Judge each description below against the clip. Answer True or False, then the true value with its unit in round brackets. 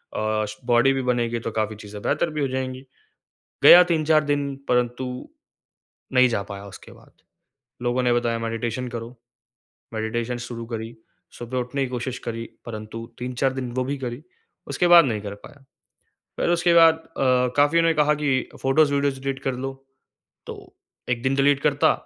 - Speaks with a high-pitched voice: False (125 Hz)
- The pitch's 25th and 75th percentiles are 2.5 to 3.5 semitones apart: True (3.2 semitones)